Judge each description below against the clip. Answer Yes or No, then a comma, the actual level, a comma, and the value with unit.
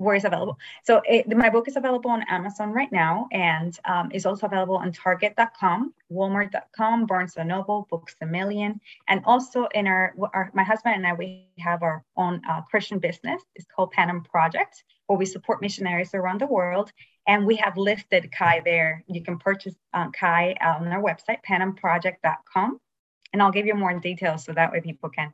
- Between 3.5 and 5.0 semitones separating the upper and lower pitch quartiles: No, average, 3.1 semitones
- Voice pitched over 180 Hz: Yes, high, 190 Hz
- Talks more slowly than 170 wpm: No, average, 190 wpm